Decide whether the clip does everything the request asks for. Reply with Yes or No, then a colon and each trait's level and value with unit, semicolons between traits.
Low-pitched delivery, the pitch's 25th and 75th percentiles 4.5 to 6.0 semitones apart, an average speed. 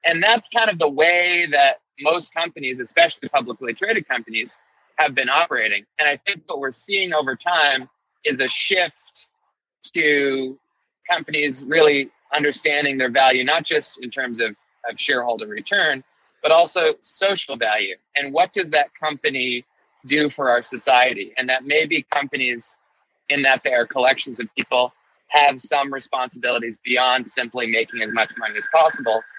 No: medium, 145 Hz; average, 5.2 semitones; average, 155 wpm